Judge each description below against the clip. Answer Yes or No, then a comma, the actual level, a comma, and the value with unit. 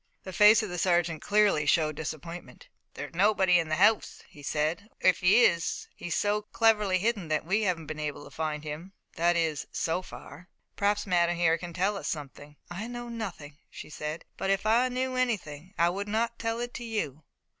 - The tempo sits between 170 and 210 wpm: Yes, average, 200 wpm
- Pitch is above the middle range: No, medium, 180 Hz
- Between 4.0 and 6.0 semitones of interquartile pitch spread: Yes, average, 5.0 semitones